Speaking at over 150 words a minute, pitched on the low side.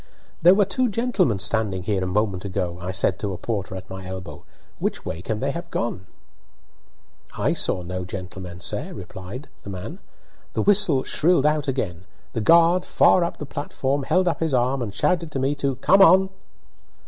Yes: average, 185 wpm; low, 125 Hz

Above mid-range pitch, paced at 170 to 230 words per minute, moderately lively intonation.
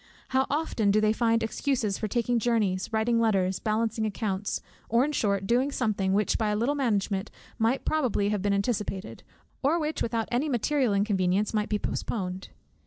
Yes: high, 220 Hz; average, 175 wpm; average, 3.2 semitones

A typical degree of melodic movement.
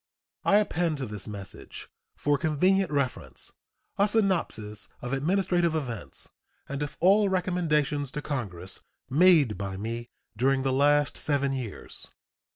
No: wide, 6.7 semitones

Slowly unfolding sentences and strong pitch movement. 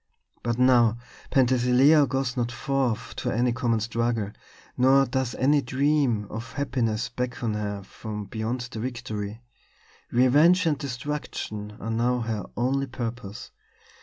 No: slow, 130 wpm; average, 2.7 semitones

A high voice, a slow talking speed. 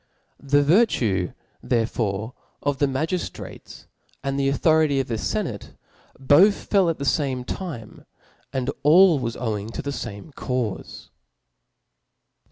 No: low, 135 Hz; slow, 130 wpm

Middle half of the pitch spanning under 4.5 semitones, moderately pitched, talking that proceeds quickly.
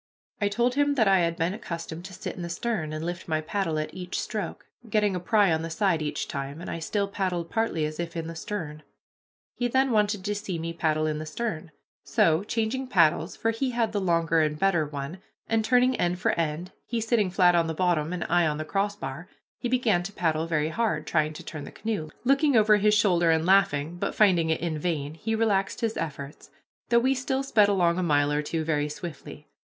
No: average, 5.0 semitones; medium, 175 Hz; fast, 225 wpm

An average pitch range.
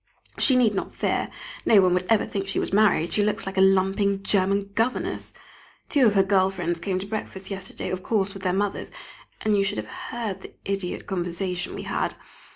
No: narrow, 1.6 semitones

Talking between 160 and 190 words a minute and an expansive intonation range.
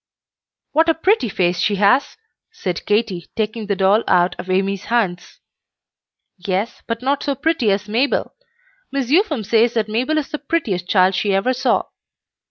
Yes: average, 165 wpm; wide, 5.9 semitones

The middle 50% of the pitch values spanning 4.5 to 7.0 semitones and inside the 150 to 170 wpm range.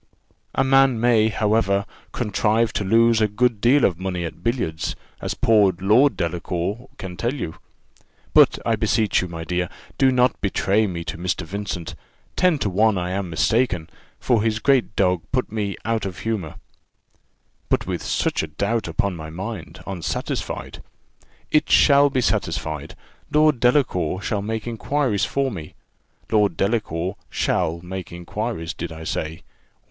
Yes: average, 4.9 semitones; average, 160 wpm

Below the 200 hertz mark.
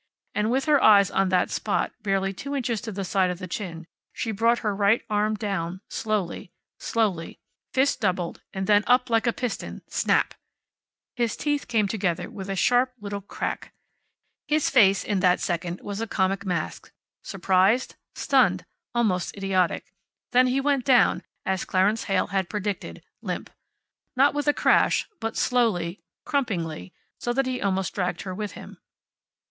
No: high, 205 Hz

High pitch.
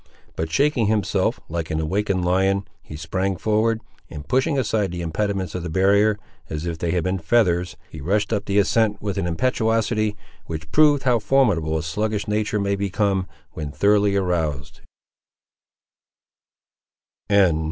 No: low, 100 Hz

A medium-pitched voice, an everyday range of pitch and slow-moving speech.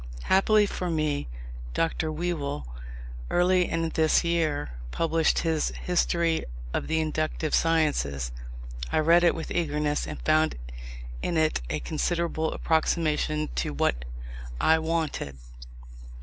No: medium, 160 Hz; narrow, 1.7 semitones; slow, 120 wpm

